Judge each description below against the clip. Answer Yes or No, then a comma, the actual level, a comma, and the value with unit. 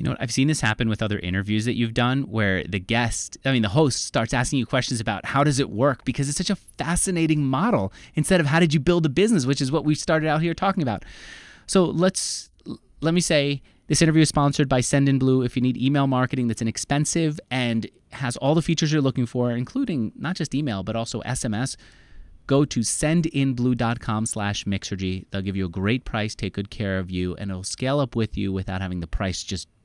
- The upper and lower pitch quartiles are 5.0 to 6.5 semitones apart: Yes, wide, 5.6 semitones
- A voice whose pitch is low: Yes, low, 130 Hz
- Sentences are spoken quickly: Yes, fast, 225 wpm